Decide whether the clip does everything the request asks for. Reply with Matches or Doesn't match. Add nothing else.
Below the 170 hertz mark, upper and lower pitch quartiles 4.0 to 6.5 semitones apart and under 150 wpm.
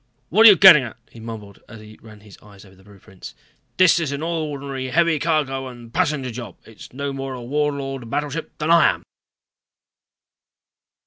Doesn't match